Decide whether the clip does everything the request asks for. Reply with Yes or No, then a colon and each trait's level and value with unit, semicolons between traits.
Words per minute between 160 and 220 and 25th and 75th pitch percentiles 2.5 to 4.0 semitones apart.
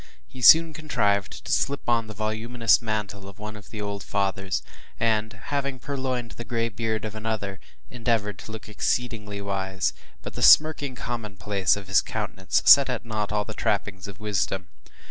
Yes: average, 170 wpm; average, 2.8 semitones